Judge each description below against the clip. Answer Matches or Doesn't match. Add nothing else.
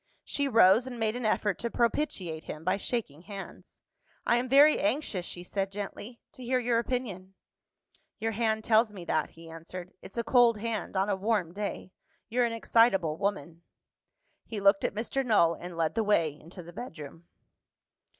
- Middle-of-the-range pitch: Doesn't match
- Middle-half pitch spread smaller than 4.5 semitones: Doesn't match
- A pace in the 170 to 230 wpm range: Matches